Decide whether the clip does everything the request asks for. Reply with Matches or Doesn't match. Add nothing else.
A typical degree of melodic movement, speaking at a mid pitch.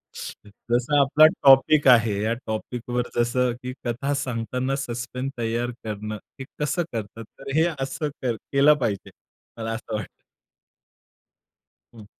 Doesn't match